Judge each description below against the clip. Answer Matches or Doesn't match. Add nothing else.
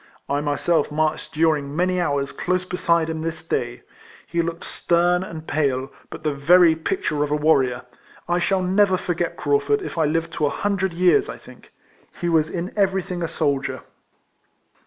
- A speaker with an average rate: Matches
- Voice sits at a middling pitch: Matches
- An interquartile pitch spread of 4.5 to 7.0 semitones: Doesn't match